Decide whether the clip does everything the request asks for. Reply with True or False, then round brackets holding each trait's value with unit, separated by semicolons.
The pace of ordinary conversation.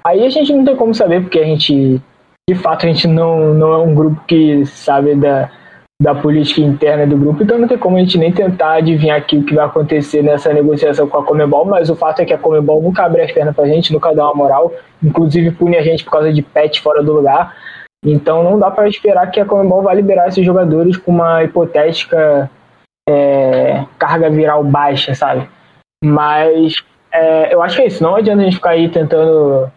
False (220 wpm)